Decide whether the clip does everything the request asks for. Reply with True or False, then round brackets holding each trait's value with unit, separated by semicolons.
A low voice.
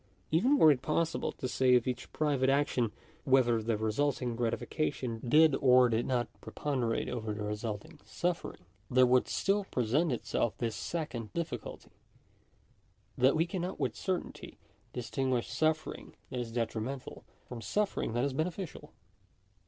True (130 Hz)